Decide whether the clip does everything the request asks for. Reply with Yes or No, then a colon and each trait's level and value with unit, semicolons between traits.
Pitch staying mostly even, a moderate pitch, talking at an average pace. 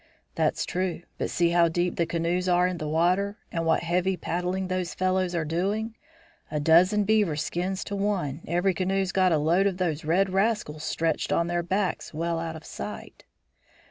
Yes: narrow, 2.3 semitones; medium, 175 Hz; average, 185 wpm